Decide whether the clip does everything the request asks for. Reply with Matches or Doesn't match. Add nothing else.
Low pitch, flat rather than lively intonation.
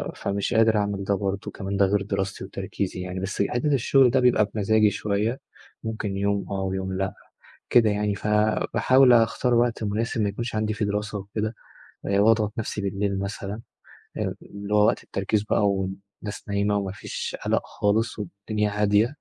Matches